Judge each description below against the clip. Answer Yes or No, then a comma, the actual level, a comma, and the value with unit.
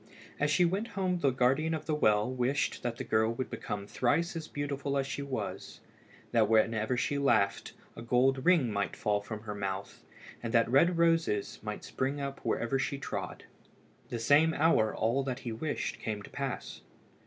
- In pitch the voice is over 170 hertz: No, low, 130 Hz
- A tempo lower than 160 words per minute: No, average, 185 wpm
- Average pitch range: Yes, average, 4.6 semitones